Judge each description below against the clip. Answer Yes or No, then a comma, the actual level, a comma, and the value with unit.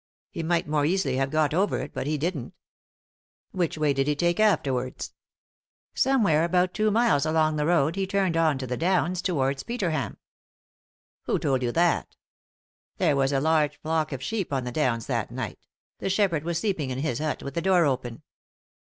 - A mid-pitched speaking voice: Yes, medium, 155 Hz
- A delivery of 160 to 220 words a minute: Yes, average, 200 wpm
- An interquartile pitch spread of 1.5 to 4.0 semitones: No, average, 4.4 semitones